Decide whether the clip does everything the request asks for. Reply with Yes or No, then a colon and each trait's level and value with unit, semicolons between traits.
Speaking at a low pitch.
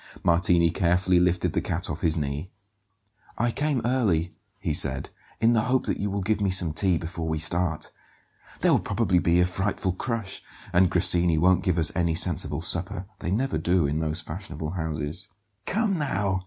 Yes: very low, 90 Hz